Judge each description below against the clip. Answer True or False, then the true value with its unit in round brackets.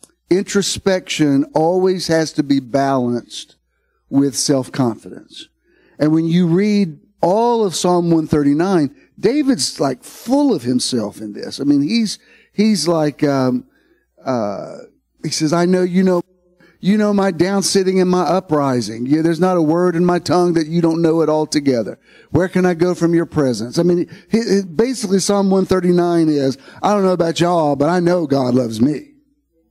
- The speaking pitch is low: False (170 Hz)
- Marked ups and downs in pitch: False (4.3 semitones)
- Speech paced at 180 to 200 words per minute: False (170 wpm)